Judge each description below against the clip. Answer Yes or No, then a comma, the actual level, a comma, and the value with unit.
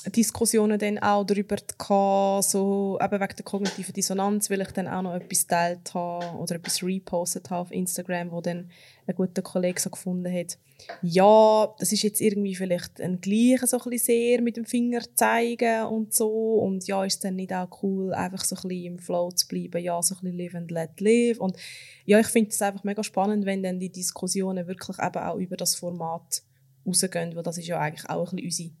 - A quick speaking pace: Yes, fast, 210 wpm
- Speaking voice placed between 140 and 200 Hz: Yes, high, 190 Hz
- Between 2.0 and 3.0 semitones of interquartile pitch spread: Yes, average, 2.7 semitones